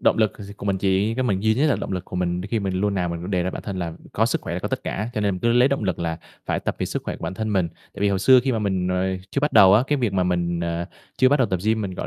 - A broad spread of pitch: No, average, 3.4 semitones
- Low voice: Yes, low, 100 Hz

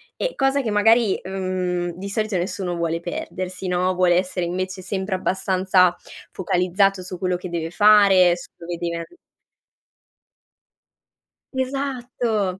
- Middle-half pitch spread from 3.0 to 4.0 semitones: No, narrow, 2.4 semitones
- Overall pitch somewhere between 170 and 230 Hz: Yes, medium, 185 Hz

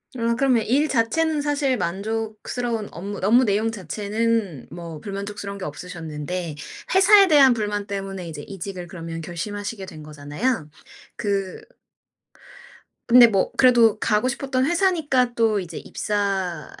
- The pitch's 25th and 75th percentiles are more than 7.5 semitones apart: No, average, 5.1 semitones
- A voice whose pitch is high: Yes, high, 210 Hz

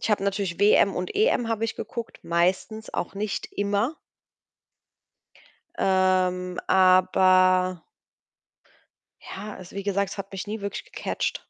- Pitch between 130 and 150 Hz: No, high, 195 Hz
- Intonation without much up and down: Yes, narrow, 2.0 semitones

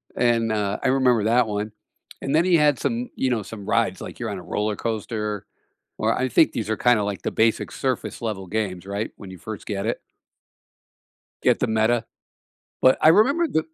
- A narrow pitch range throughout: No, average, 3.4 semitones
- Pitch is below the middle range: Yes, low, 110 Hz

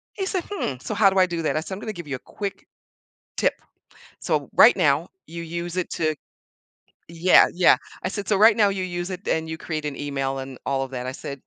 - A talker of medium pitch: Yes, medium, 170 Hz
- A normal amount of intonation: Yes, average, 5.0 semitones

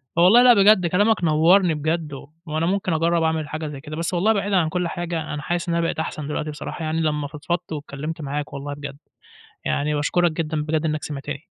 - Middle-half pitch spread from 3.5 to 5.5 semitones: No, narrow, 2.6 semitones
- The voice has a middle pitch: Yes, medium, 160 Hz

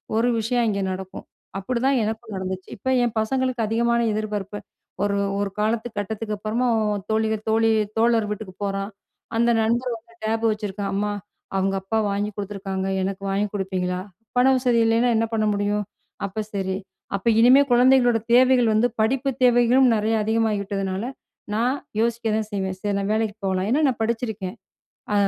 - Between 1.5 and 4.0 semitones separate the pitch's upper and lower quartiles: Yes, average, 2.9 semitones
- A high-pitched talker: Yes, high, 220 Hz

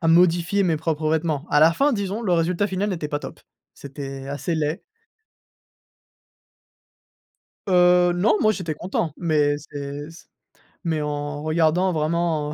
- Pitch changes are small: No, average, 3.2 semitones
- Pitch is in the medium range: Yes, medium, 165 Hz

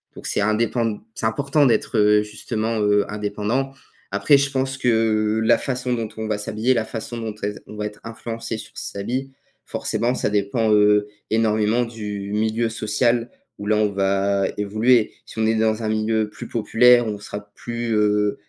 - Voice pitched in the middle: No, low, 110 Hz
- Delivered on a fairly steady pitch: Yes, narrow, 2.0 semitones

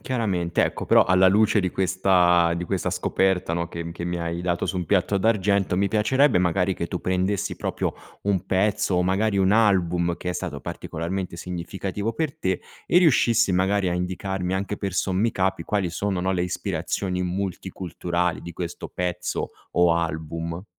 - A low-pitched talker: Yes, very low, 95 Hz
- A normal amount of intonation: No, narrow, 2.1 semitones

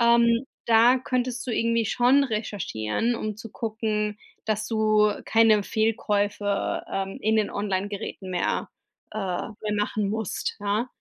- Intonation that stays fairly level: Yes, narrow, 2.0 semitones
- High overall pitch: Yes, high, 215 Hz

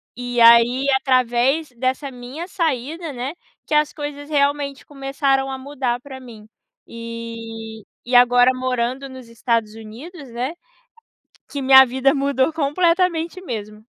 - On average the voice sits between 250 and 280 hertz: Yes, very high, 260 Hz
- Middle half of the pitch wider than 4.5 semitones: No, average, 3.1 semitones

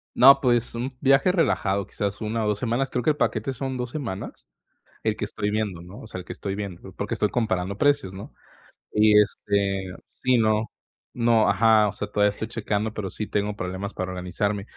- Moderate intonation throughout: Yes, average, 3.0 semitones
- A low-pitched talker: Yes, low, 105 Hz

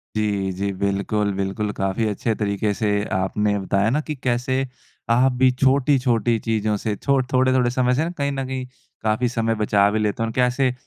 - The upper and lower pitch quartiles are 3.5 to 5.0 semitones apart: Yes, average, 3.8 semitones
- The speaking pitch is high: No, low, 115 Hz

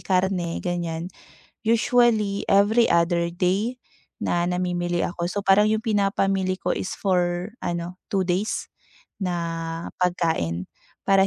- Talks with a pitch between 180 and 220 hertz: Yes, medium, 185 Hz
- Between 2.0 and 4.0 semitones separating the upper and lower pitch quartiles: Yes, narrow, 2.4 semitones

